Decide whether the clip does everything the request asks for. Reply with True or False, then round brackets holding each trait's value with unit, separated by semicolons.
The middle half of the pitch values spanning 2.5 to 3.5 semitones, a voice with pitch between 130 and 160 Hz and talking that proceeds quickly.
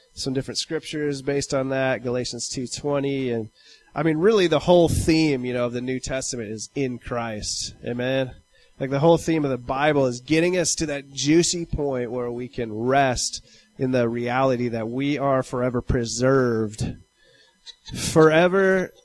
False (3.2 semitones; 135 Hz; 165 wpm)